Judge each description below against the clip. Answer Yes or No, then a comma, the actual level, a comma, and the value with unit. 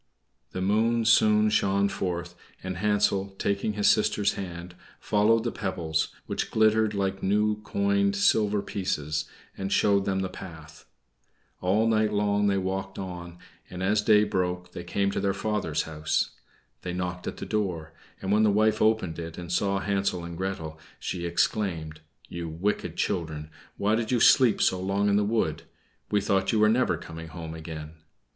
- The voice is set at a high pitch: No, very low, 95 Hz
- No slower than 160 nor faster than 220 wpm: Yes, average, 170 wpm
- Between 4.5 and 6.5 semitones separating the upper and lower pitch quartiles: No, average, 3.4 semitones